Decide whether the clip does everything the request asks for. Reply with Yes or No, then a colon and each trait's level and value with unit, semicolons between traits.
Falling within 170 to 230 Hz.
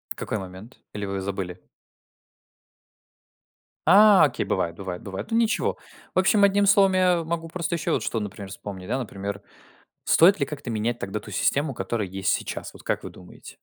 No: low, 115 Hz